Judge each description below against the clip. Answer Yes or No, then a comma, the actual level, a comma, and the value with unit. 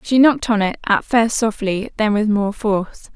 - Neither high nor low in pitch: No, high, 215 Hz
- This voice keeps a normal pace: No, fast, 210 wpm